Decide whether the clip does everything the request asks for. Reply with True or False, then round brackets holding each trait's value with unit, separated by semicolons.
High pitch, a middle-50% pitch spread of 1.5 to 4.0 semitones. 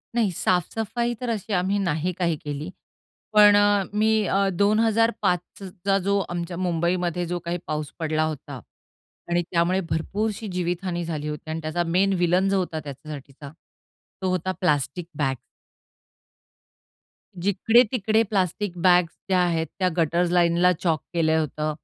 False (180 Hz; 3.5 semitones)